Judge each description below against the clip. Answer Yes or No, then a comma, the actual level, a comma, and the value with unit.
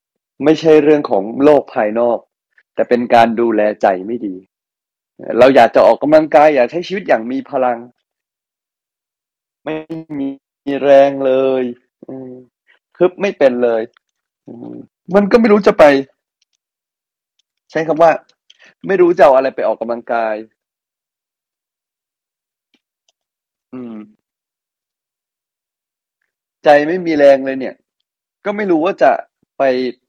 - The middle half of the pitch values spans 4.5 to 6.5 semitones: Yes, average, 4.9 semitones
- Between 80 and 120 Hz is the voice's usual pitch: No, medium, 140 Hz